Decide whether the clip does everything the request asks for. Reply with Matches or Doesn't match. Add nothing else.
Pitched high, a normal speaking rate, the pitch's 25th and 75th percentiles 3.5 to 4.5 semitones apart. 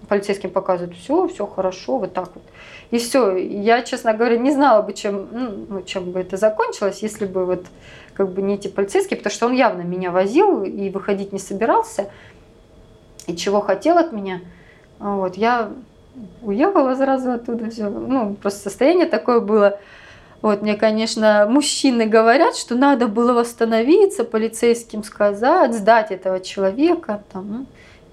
Matches